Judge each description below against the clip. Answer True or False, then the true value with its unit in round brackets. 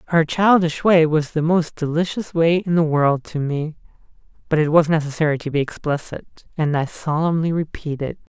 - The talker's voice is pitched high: False (160 Hz)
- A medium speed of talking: True (170 wpm)